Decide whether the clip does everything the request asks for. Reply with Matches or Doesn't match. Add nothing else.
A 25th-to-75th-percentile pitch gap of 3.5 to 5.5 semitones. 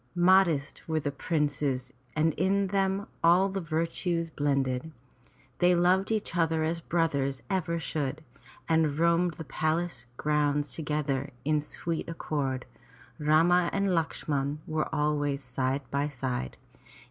Doesn't match